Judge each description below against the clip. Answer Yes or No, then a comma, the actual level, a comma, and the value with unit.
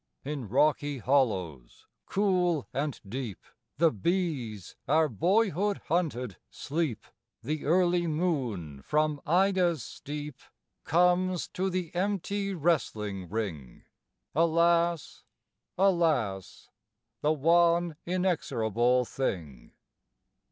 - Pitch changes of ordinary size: No, wide, 6.6 semitones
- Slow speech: Yes, slow, 90 wpm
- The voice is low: No, medium, 155 Hz